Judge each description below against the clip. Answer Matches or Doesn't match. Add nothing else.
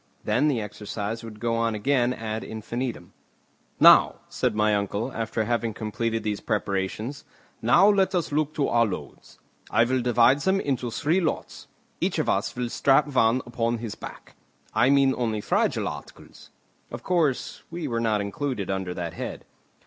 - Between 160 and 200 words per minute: Matches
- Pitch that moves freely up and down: Doesn't match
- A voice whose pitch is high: Doesn't match